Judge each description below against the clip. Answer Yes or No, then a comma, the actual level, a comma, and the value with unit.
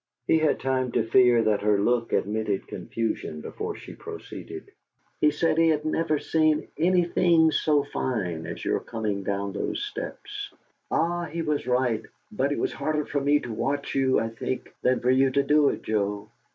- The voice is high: No, low, 135 Hz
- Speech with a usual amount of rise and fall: No, wide, 5.8 semitones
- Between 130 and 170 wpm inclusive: No, average, 180 wpm